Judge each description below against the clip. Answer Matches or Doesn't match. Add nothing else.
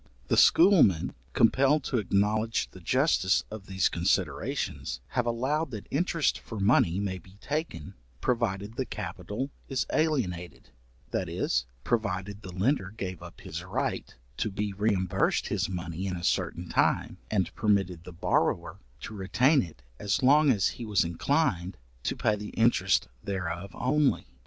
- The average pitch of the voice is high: Doesn't match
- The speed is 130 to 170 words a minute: Matches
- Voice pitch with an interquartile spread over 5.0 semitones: Matches